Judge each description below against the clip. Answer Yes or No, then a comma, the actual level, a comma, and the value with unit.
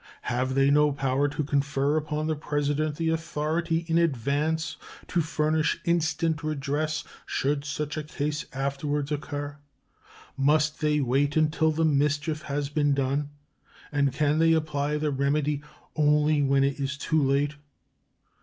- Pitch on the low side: No, medium, 150 Hz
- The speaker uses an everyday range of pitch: No, narrow, 1.6 semitones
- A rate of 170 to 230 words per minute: No, average, 145 wpm